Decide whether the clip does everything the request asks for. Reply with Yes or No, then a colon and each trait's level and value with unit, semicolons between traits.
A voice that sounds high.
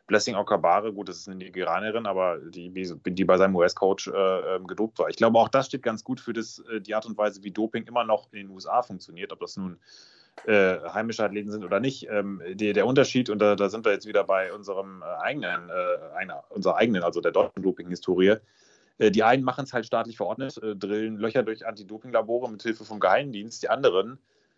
No: low, 110 Hz